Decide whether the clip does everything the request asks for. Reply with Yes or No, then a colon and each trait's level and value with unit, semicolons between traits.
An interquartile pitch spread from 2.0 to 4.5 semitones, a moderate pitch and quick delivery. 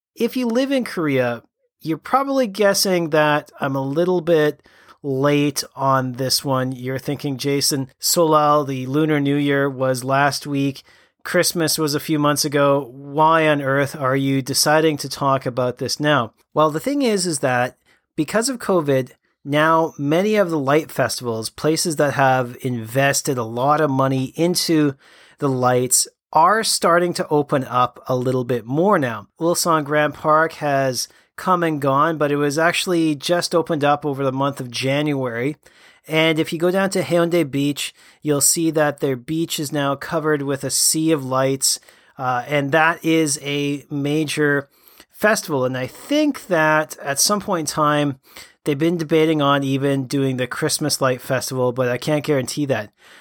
No: average, 3.2 semitones; medium, 145 Hz; average, 170 wpm